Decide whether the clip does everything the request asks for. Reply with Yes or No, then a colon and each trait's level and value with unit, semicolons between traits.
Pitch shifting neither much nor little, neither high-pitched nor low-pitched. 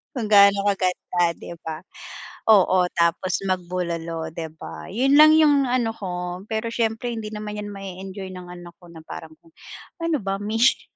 No: average, 4.1 semitones; high, 195 Hz